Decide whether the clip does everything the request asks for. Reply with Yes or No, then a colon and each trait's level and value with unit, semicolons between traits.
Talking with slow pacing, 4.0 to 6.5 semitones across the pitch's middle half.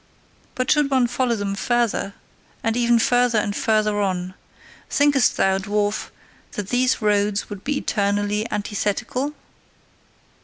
No: slow, 125 wpm; average, 3.3 semitones